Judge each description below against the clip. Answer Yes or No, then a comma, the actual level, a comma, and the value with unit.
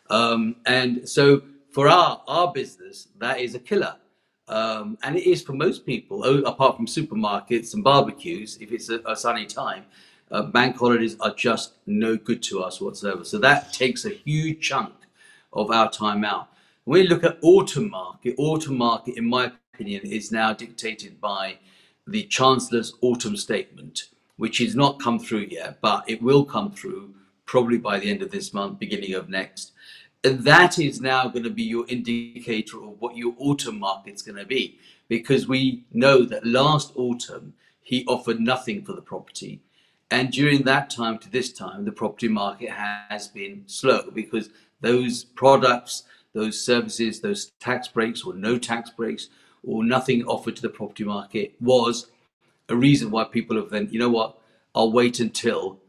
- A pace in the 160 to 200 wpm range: Yes, average, 175 wpm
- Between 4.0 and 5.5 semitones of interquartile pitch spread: No, average, 3.4 semitones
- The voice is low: Yes, low, 120 Hz